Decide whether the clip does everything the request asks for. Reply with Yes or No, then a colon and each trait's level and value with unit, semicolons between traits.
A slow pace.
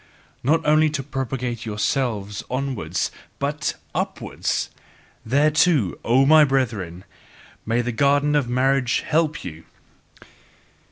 Yes: slow, 105 wpm